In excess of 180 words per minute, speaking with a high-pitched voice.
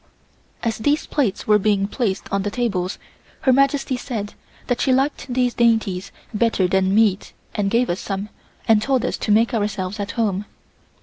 No: average, 175 wpm; high, 215 Hz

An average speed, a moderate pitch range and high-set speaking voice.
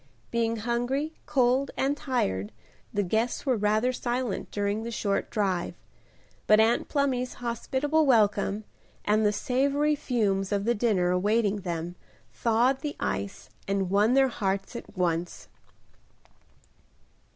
No: slow, 130 wpm; average, 4.2 semitones; high, 225 Hz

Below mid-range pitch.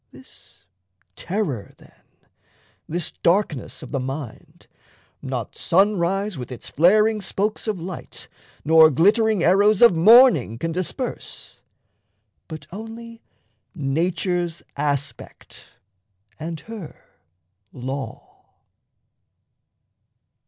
No: medium, 175 Hz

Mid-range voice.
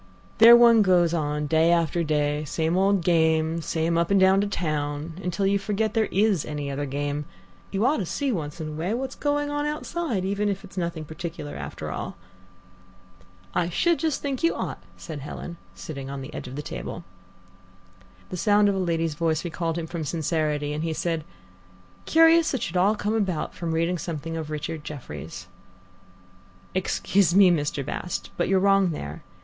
Yes: medium, 170 Hz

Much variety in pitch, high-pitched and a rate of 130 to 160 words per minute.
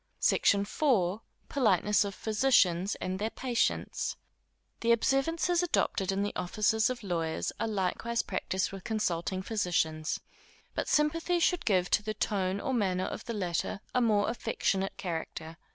No: average, 4.1 semitones; high, 205 Hz; average, 145 wpm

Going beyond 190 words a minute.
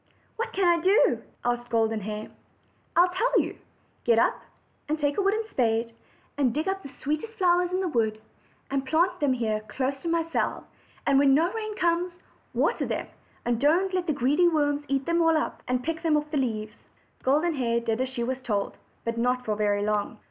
Yes: fast, 205 wpm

